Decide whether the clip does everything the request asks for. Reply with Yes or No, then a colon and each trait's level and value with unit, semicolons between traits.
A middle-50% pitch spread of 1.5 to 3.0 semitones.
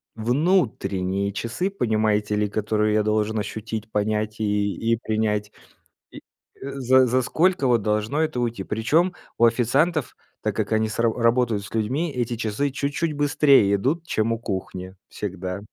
No: average, 3.8 semitones